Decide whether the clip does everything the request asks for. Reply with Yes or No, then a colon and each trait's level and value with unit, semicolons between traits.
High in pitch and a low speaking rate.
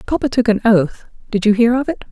No: high, 230 Hz; fast, 225 wpm